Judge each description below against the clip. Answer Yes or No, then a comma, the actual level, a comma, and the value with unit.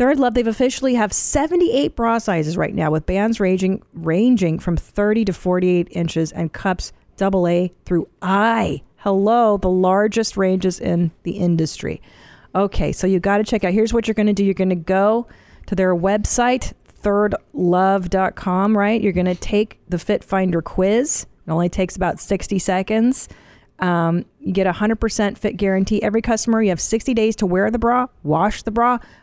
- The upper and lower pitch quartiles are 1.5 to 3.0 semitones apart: No, average, 3.4 semitones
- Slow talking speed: No, average, 180 wpm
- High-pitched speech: Yes, high, 195 Hz